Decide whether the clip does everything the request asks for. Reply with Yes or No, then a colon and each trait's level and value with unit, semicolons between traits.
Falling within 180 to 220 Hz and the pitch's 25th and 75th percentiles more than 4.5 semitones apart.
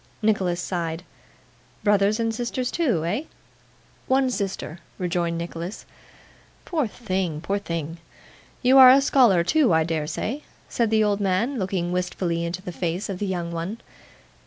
Yes: high, 190 Hz; average, 4.9 semitones